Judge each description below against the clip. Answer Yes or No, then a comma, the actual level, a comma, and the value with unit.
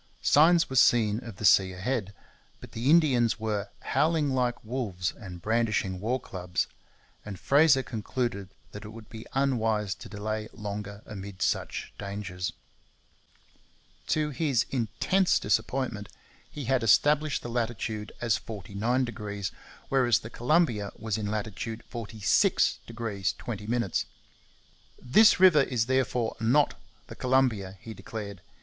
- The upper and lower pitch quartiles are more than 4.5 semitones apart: No, average, 3.9 semitones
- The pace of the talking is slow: Yes, slow, 125 wpm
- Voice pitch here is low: Yes, low, 115 Hz